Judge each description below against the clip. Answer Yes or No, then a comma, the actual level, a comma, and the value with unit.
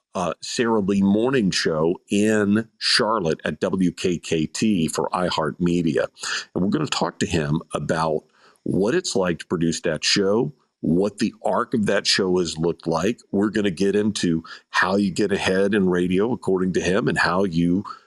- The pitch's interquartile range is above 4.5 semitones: No, average, 2.7 semitones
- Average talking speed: Yes, average, 175 wpm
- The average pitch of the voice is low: Yes, very low, 95 Hz